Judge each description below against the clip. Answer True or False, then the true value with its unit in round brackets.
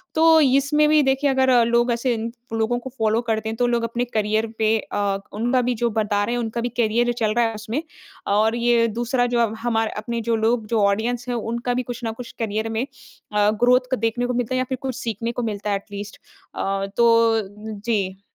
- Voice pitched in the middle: False (230 Hz)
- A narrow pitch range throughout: True (1.9 semitones)